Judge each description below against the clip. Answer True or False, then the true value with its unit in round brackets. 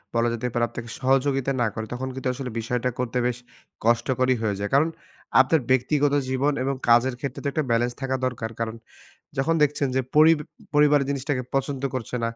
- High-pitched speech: False (130 Hz)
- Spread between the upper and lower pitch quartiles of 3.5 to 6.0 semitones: False (2.6 semitones)